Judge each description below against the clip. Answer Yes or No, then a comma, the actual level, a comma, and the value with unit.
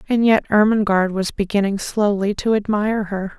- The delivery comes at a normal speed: Yes, average, 160 wpm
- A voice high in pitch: Yes, high, 205 Hz